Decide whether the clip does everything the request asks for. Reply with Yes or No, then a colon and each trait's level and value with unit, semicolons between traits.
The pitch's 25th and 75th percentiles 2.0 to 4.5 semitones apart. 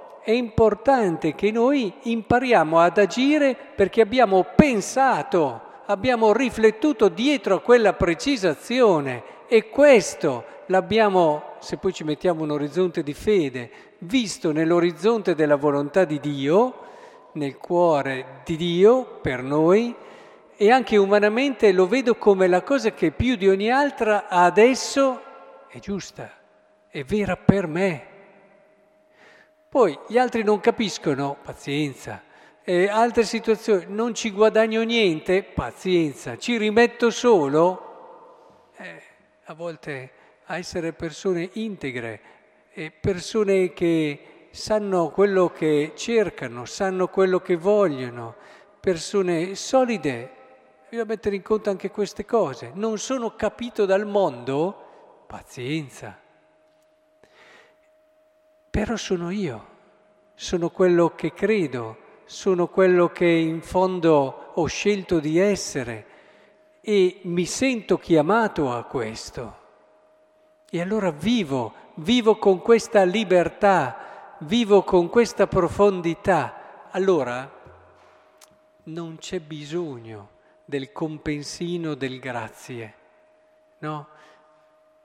No: wide, 5.6 semitones